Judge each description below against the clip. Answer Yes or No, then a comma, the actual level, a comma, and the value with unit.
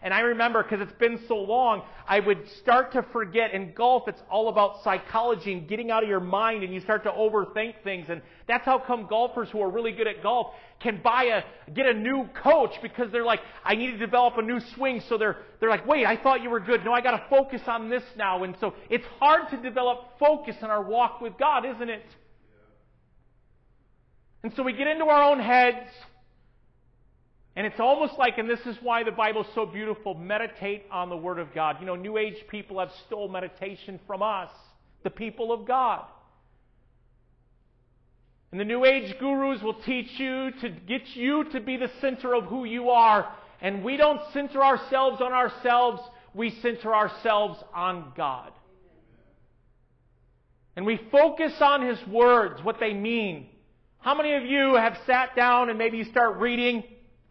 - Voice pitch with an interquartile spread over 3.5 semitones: No, average, 3.0 semitones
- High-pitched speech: Yes, high, 230 Hz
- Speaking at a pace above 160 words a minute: Yes, average, 195 wpm